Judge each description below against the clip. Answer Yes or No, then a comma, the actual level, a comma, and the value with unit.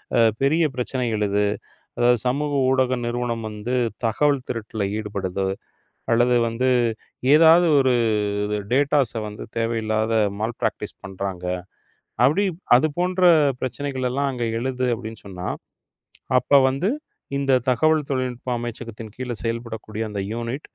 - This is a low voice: Yes, low, 120 Hz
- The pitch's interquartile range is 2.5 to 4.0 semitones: Yes, average, 3.4 semitones